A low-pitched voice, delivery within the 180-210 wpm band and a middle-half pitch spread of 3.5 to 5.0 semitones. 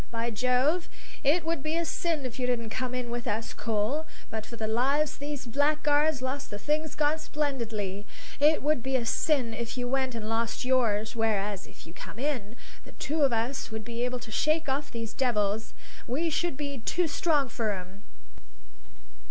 No: very high, 255 Hz; average, 190 wpm; average, 4.6 semitones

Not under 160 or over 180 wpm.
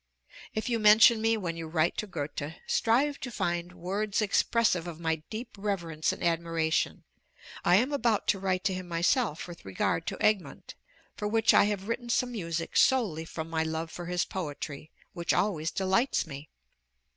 Yes: average, 175 wpm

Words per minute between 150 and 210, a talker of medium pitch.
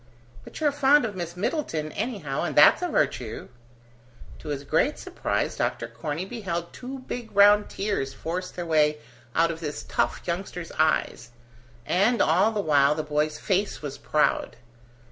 Yes: average, 160 wpm; medium, 170 Hz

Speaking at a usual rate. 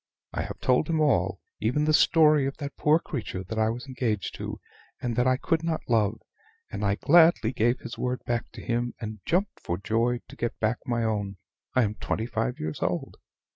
No: fast, 210 wpm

